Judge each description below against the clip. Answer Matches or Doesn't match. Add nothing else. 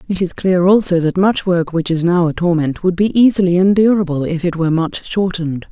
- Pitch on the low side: Doesn't match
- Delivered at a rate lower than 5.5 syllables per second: Doesn't match